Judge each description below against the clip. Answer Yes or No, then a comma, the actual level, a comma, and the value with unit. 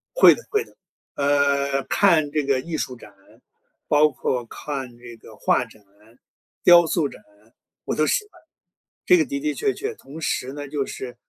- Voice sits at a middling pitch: Yes, medium, 145 Hz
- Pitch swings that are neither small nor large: Yes, average, 4.3 semitones